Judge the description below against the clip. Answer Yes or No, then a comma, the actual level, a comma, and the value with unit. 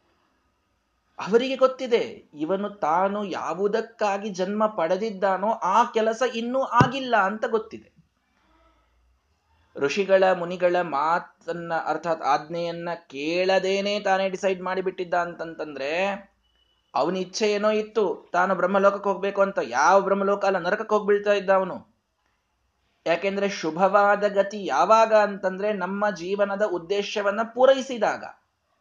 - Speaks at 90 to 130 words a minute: Yes, average, 100 wpm